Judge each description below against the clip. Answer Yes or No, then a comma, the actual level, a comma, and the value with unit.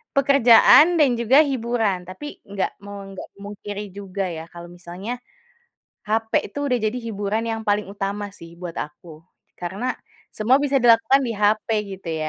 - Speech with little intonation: No, average, 3.2 semitones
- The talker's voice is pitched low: No, high, 210 Hz